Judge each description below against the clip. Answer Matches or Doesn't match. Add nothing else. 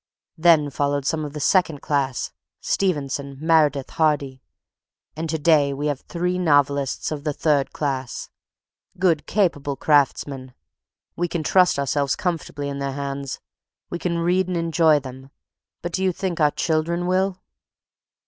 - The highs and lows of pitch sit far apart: Doesn't match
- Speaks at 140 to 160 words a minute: Matches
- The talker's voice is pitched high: Doesn't match